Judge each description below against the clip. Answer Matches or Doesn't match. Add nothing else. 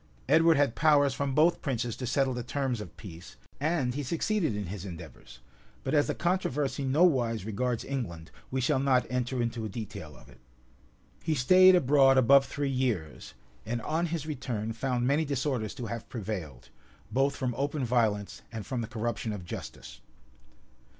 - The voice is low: Matches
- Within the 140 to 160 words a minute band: Doesn't match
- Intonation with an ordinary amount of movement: Matches